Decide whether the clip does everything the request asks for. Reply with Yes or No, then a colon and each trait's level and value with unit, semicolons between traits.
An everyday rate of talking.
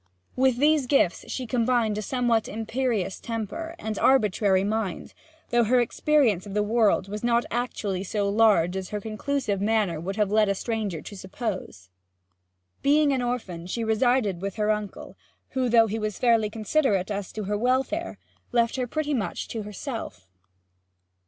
Yes: average, 165 wpm